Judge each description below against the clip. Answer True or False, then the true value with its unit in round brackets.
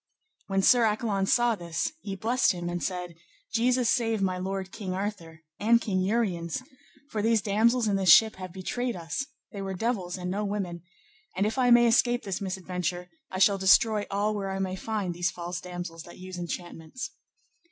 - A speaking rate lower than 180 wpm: False (185 wpm)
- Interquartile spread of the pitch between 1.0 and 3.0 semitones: False (3.7 semitones)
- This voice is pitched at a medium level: False (195 Hz)